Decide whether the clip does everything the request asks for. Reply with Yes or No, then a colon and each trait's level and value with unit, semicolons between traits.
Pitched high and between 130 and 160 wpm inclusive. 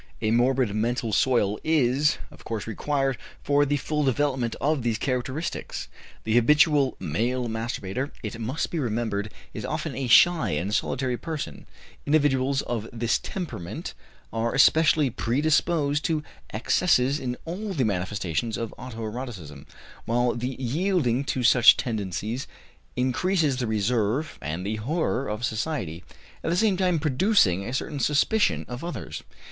No: low, 125 Hz; average, 140 wpm